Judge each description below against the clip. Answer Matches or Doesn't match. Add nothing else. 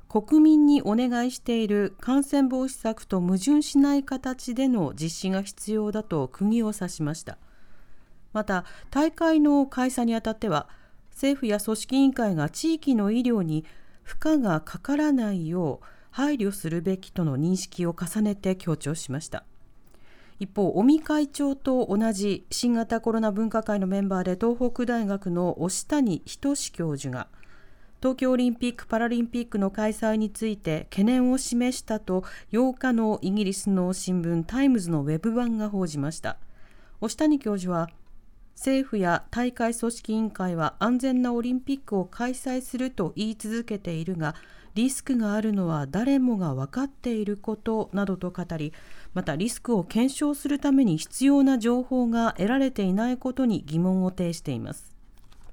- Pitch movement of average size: Doesn't match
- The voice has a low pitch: Doesn't match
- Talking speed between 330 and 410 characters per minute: Doesn't match